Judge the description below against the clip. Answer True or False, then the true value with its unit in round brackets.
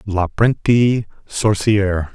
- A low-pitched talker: True (100 Hz)